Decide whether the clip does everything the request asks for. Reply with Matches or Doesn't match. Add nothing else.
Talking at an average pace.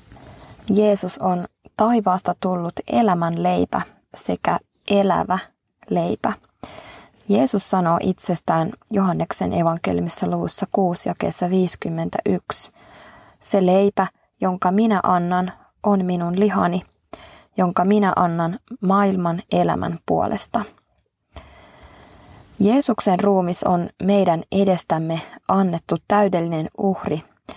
Doesn't match